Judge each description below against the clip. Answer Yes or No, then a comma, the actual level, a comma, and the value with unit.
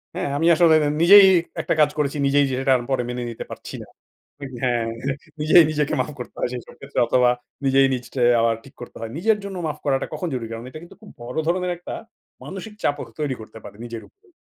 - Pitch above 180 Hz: No, low, 135 Hz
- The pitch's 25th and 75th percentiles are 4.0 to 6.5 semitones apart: Yes, average, 5.2 semitones